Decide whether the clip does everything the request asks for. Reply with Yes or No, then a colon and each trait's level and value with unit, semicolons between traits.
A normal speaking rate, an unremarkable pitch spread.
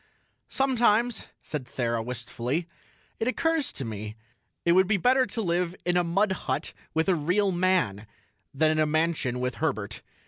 No: average, 165 wpm; wide, 7.8 semitones